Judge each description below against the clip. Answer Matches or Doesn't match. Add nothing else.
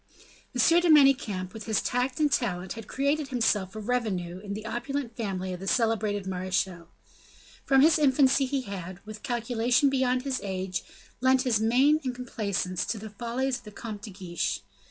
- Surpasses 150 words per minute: Matches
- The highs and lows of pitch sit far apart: Doesn't match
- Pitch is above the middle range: Matches